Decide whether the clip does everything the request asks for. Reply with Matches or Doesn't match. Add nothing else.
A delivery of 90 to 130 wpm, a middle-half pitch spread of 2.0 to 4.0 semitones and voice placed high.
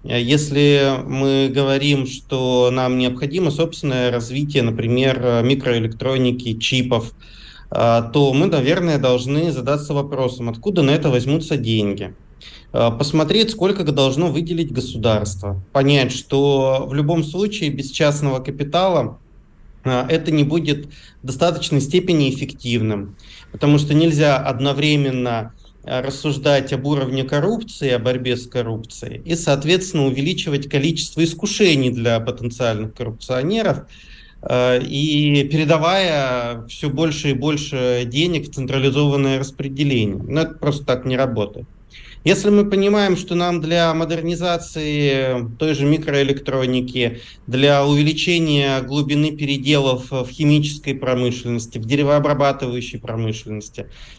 Doesn't match